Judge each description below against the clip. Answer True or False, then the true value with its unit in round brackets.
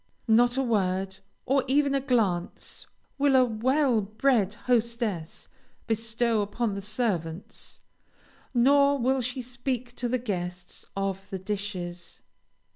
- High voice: True (230 Hz)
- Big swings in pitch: False (4.5 semitones)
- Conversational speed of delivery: False (120 wpm)